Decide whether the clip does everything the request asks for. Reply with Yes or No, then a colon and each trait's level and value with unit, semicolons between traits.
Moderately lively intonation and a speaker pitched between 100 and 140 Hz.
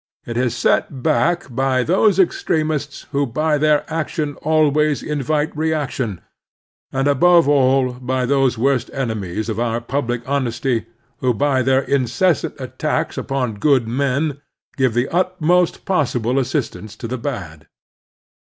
Yes: average, 3.8 semitones; low, 135 Hz